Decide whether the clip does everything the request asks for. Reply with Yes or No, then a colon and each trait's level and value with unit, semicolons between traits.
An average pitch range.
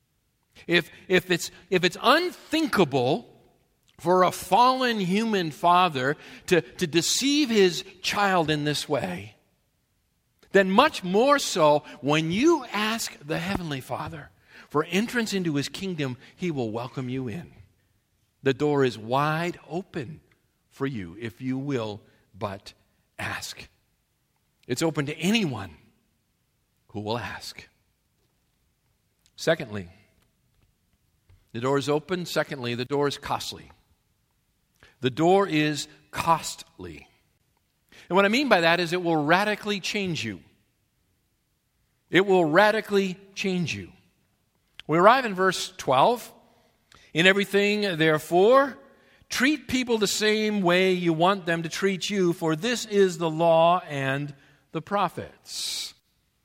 No: wide, 7.3 semitones